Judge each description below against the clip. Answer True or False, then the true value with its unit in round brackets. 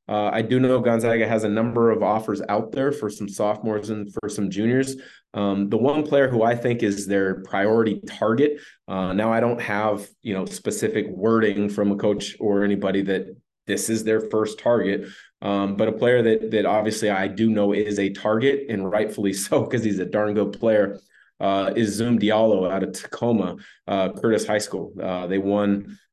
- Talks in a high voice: False (105 Hz)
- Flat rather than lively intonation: True (2.0 semitones)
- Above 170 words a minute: True (200 wpm)